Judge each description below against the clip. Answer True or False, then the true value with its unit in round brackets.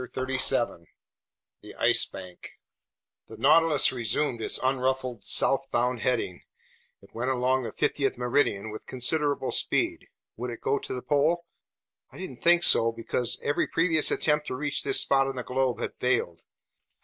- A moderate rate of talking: True (155 wpm)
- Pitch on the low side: True (130 Hz)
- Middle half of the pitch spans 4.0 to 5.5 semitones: False (3.3 semitones)